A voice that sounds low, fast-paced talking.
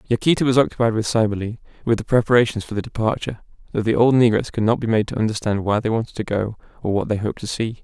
Yes: low, 110 Hz; fast, 245 wpm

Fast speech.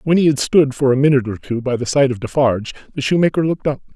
Yes: fast, 275 wpm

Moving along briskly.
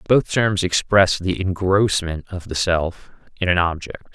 No: average, 160 wpm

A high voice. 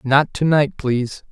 No: medium, 140 Hz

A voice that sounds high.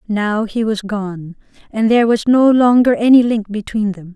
Yes: high, 220 Hz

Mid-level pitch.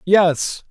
Yes: medium, 175 Hz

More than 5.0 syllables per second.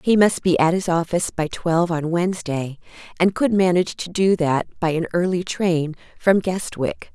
No: 4.9 syllables/s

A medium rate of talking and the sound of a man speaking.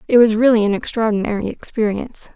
No: average, 155 wpm; female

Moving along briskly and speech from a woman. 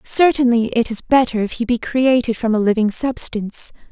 No: average, 185 wpm; female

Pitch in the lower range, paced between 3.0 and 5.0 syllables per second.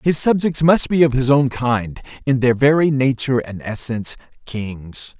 Yes: low, 130 Hz; 4.6 syllables/s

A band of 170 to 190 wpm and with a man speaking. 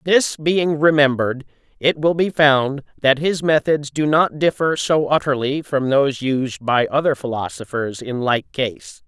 No: average, 160 wpm; male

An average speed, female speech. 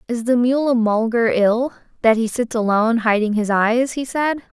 Yes: average, 185 wpm; female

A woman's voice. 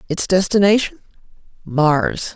Yes: female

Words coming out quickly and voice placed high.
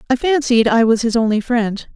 Yes: fast, 215 wpm; high, 235 Hz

